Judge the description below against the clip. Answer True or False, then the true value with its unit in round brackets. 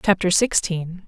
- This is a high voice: False (180 Hz)